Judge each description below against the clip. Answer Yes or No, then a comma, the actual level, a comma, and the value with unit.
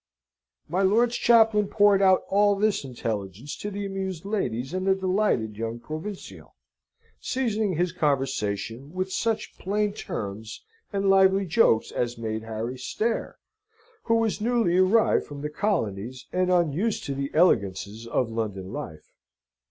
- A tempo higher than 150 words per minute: No, average, 140 wpm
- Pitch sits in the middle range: Yes, medium, 180 Hz